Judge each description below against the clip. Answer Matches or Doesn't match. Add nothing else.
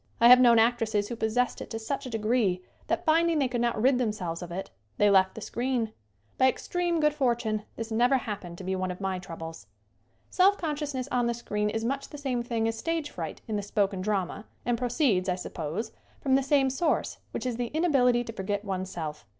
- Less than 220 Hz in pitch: Doesn't match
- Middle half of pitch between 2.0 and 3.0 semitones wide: Doesn't match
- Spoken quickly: Matches